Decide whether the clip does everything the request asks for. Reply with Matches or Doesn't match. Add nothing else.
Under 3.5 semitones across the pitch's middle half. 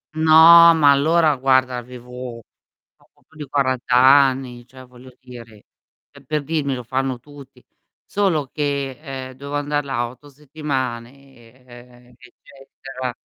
Matches